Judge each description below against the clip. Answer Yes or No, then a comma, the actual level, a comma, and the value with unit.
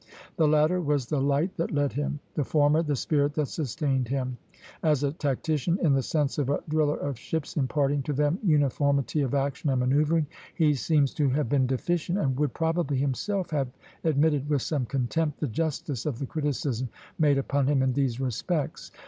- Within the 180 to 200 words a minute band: Yes, average, 190 wpm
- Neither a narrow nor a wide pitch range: No, narrow, 2.2 semitones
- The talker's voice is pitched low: No, medium, 145 Hz